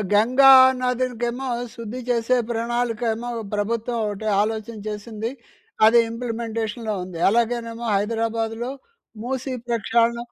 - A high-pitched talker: Yes, high, 230 Hz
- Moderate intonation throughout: No, narrow, 1.4 semitones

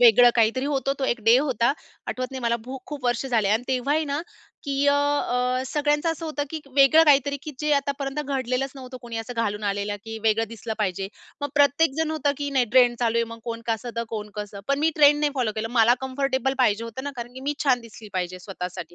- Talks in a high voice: Yes, very high, 255 Hz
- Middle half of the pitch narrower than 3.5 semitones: No, average, 3.8 semitones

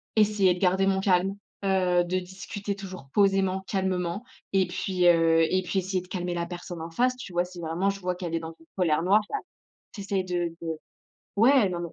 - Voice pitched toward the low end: No, medium, 185 Hz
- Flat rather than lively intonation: Yes, narrow, 1.9 semitones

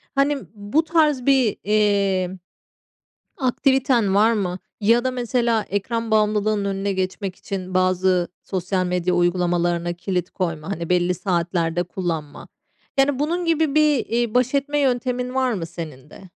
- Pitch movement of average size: No, wide, 5.8 semitones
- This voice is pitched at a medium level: No, high, 200 Hz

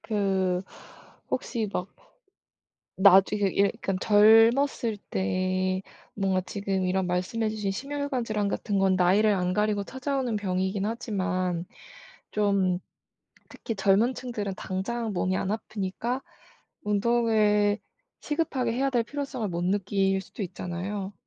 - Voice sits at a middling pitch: No, high, 205 Hz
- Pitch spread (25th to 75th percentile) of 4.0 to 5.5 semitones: No, average, 3.2 semitones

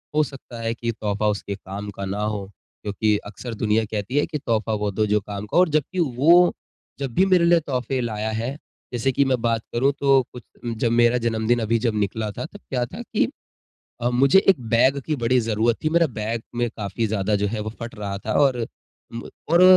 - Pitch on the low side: Yes, low, 115 Hz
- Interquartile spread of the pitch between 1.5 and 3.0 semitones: No, average, 4.0 semitones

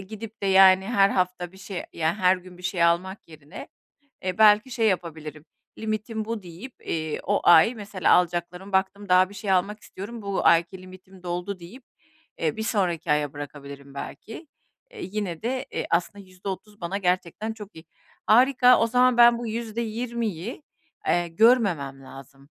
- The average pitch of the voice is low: No, high, 190 Hz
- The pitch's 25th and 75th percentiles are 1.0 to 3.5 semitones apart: No, average, 4.1 semitones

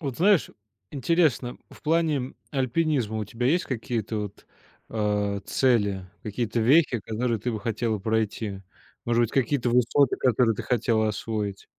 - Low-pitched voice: Yes, low, 115 Hz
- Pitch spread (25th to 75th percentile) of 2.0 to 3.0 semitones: No, average, 3.6 semitones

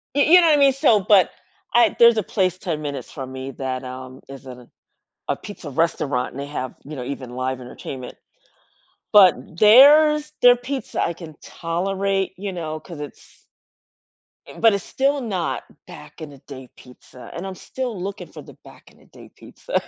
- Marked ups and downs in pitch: Yes, wide, 8.5 semitones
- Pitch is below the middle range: No, medium, 175 Hz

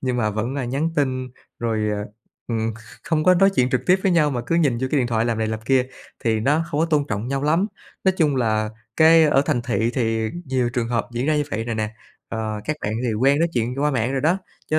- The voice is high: No, low, 125 Hz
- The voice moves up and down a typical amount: Yes, average, 4.8 semitones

